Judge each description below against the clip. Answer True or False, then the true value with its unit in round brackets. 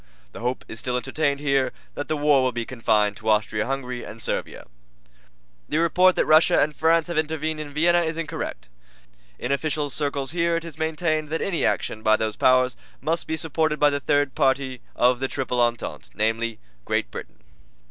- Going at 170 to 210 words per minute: True (190 wpm)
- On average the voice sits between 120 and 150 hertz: True (140 Hz)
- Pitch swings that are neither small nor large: True (4.3 semitones)